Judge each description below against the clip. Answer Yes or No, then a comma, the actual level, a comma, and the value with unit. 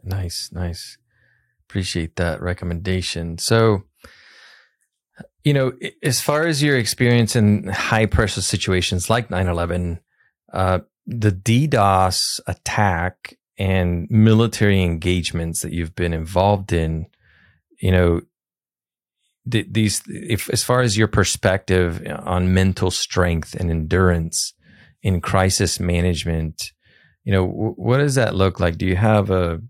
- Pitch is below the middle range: Yes, very low, 95 Hz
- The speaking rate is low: Yes, slow, 125 wpm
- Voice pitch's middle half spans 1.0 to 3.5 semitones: No, average, 3.9 semitones